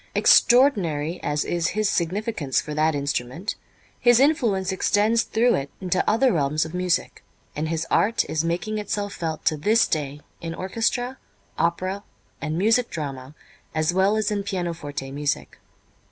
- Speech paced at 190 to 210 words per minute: No, average, 150 wpm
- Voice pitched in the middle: Yes, medium, 180 Hz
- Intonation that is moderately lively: No, wide, 5.7 semitones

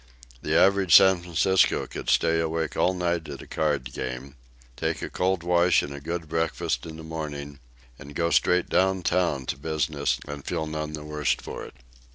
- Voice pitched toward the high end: No, very low, 80 Hz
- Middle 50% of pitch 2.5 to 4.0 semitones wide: Yes, average, 3.1 semitones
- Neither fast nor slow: Yes, average, 185 wpm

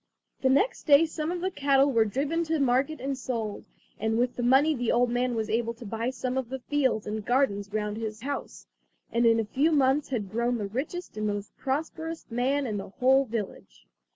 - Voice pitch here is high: Yes, very high, 250 Hz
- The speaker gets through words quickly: Yes, fast, 210 wpm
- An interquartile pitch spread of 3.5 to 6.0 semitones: Yes, average, 3.9 semitones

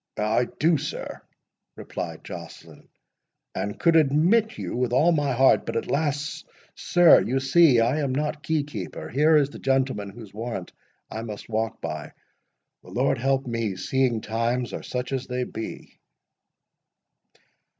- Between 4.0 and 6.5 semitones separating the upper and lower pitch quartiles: Yes, average, 4.3 semitones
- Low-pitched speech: Yes, low, 130 Hz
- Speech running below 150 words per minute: Yes, average, 140 wpm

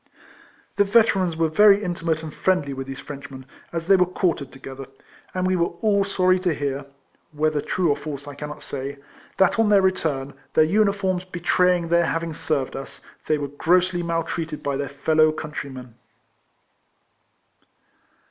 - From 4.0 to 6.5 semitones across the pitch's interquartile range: Yes, average, 4.5 semitones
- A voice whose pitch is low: No, medium, 165 Hz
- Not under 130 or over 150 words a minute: No, average, 165 wpm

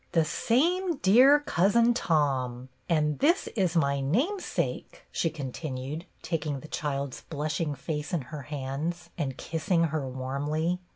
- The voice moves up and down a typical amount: Yes, average, 4.5 semitones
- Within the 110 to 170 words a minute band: Yes, average, 140 wpm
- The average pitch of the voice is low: No, medium, 155 Hz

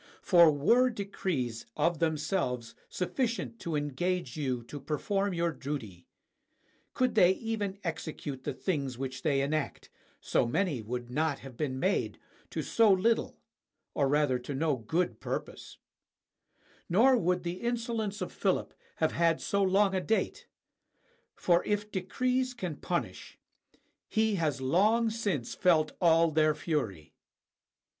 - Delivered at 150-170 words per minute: No, slow, 135 wpm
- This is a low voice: No, medium, 170 Hz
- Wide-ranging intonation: Yes, wide, 6.2 semitones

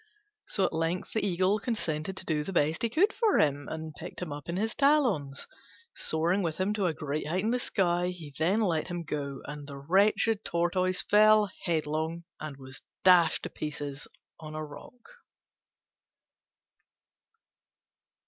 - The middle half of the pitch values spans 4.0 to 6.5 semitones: Yes, average, 4.6 semitones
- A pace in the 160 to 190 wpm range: Yes, average, 165 wpm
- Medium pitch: Yes, medium, 170 Hz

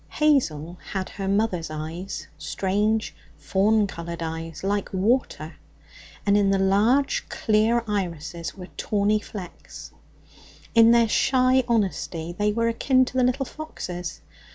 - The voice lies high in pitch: Yes, high, 200 Hz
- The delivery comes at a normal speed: No, slow, 130 wpm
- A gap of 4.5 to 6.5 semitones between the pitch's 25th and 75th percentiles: Yes, average, 4.8 semitones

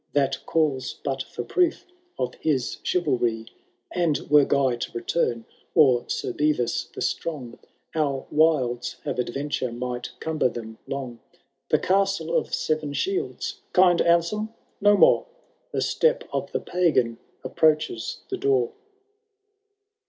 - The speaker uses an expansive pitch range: Yes, wide, 5.9 semitones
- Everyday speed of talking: No, slow, 130 wpm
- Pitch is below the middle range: No, medium, 150 Hz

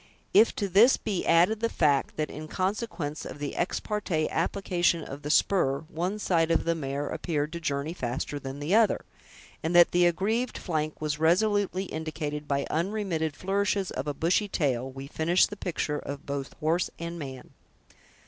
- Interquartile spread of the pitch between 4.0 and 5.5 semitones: Yes, average, 4.5 semitones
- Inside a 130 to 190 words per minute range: Yes, average, 175 wpm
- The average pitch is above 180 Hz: No, medium, 165 Hz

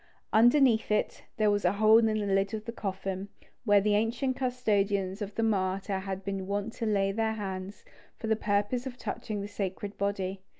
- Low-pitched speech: No, high, 205 Hz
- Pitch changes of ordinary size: No, narrow, 2.2 semitones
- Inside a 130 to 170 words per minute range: No, average, 195 wpm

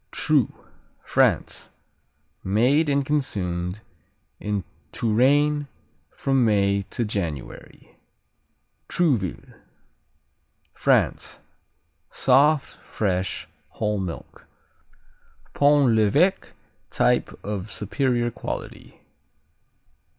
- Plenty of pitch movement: Yes, wide, 6.2 semitones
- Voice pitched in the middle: No, low, 115 Hz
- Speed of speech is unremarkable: No, slow, 70 wpm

